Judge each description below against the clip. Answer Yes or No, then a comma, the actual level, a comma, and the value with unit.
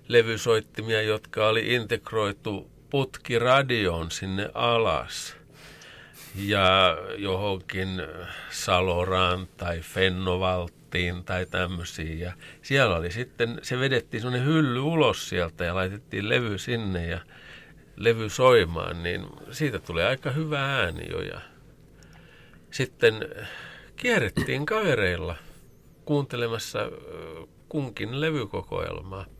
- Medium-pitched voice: No, low, 105 Hz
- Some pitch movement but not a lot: No, wide, 5.9 semitones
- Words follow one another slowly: Yes, slow, 90 wpm